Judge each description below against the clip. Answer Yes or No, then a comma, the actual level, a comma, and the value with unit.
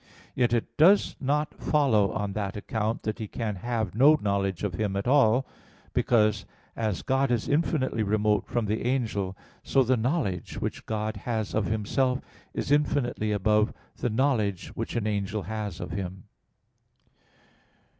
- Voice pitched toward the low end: Yes, low, 110 Hz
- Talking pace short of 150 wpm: No, average, 155 wpm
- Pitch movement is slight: No, average, 3.6 semitones